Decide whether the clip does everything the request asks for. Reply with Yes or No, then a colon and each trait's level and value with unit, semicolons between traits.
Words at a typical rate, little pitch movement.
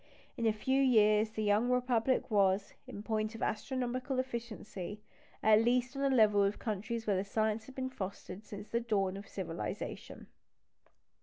No: average, 165 wpm; average, 3.2 semitones